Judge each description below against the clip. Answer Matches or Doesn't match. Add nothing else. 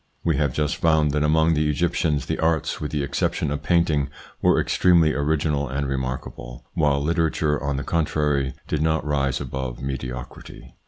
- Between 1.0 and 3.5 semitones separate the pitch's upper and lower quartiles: Matches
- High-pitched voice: Doesn't match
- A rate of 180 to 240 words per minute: Doesn't match